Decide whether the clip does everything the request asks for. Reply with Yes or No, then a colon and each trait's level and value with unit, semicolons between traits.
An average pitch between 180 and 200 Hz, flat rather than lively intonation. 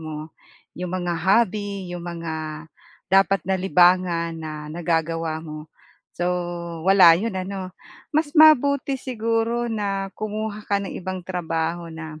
No: medium, 185 Hz; average, 3.7 semitones